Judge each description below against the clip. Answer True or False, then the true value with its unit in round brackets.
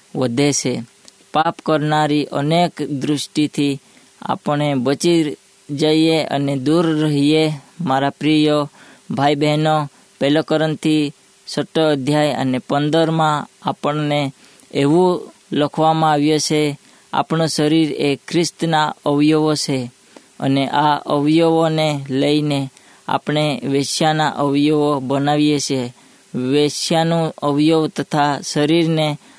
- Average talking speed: False (90 wpm)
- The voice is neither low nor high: True (150 Hz)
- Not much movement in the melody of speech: True (1.5 semitones)